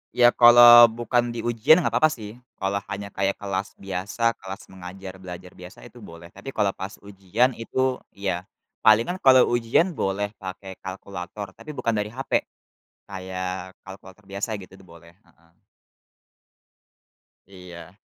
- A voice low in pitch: Yes, low, 100 Hz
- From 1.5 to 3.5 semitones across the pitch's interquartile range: No, average, 4.0 semitones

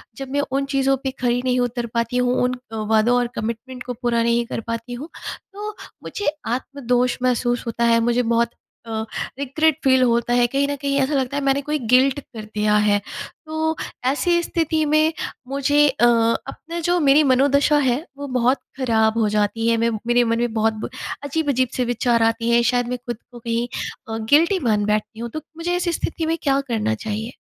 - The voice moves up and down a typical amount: Yes, average, 3.3 semitones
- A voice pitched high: Yes, very high, 250 Hz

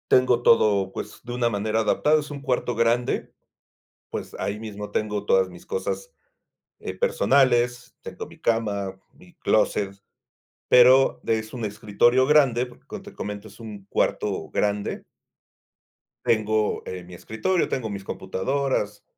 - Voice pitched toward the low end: Yes, low, 110 Hz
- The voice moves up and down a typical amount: Yes, average, 3.5 semitones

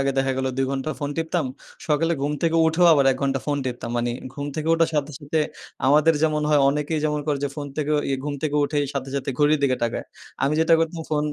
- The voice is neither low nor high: Yes, medium, 150 Hz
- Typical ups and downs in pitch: No, narrow, 2.1 semitones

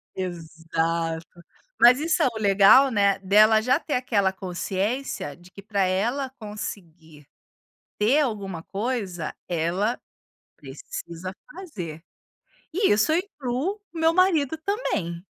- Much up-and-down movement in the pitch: Yes, wide, 7.0 semitones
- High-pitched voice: Yes, high, 205 Hz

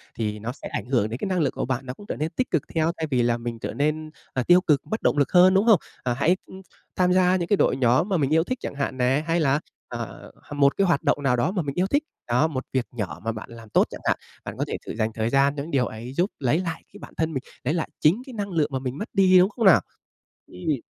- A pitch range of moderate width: No, wide, 6.3 semitones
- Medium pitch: Yes, medium, 150 Hz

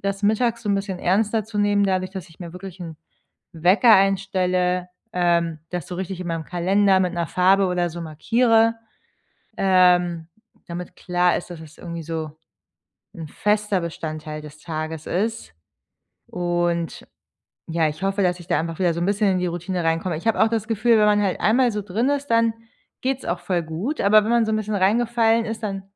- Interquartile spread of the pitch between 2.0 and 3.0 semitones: No, average, 3.6 semitones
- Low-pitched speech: No, medium, 185 Hz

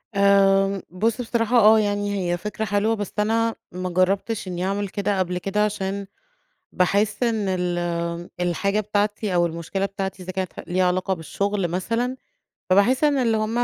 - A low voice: No, high, 200 Hz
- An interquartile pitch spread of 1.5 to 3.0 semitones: Yes, narrow, 2.6 semitones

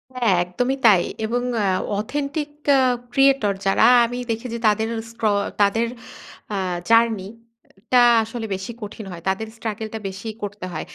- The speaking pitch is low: No, high, 225 Hz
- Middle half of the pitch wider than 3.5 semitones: No, average, 3.1 semitones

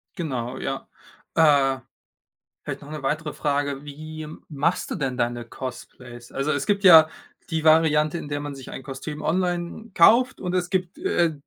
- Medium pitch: Yes, medium, 150 Hz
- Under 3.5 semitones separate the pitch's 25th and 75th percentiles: No, average, 3.9 semitones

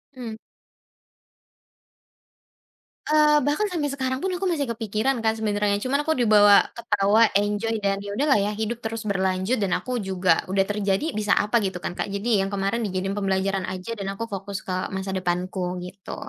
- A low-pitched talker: No, high, 205 Hz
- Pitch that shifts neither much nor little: Yes, average, 3.2 semitones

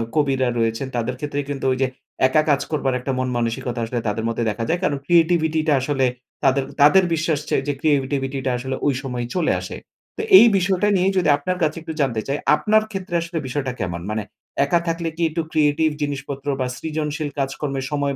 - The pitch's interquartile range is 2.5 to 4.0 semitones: Yes, average, 3.6 semitones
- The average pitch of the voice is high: No, medium, 145 Hz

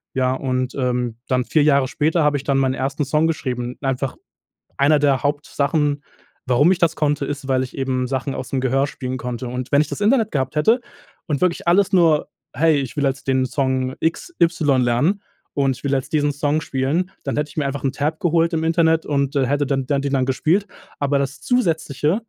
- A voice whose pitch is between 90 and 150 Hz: Yes, medium, 140 Hz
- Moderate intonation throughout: Yes, average, 3.0 semitones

